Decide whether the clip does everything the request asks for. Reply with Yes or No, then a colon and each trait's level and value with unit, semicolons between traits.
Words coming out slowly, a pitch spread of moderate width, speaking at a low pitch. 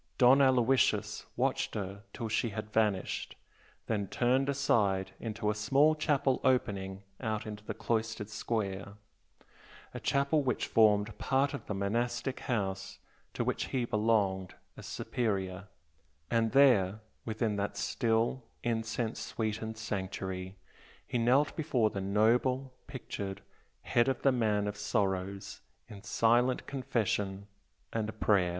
Yes: slow, 130 wpm; average, 3.7 semitones; low, 110 Hz